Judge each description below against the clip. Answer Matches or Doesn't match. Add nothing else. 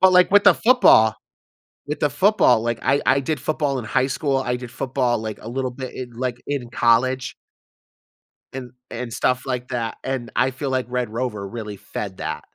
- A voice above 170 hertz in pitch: Doesn't match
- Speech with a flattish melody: Matches